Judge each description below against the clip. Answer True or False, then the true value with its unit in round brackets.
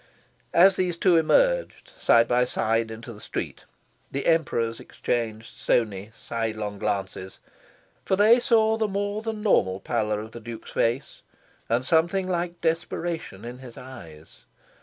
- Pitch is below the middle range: True (125 Hz)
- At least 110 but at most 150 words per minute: True (145 wpm)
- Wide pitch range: True (8.5 semitones)